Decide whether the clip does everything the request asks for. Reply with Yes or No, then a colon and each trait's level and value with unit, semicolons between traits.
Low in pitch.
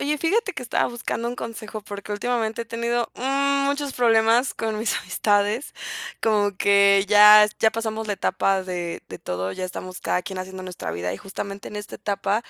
No: high, 210 Hz